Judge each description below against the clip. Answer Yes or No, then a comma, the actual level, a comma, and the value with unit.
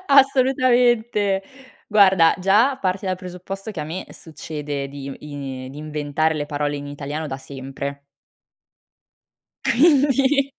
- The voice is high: No, medium, 170 Hz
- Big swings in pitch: Yes, wide, 8.0 semitones